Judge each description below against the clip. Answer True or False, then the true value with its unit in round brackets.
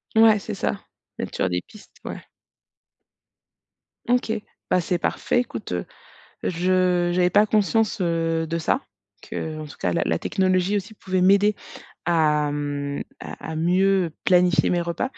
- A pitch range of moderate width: True (3.5 semitones)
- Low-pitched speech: False (180 Hz)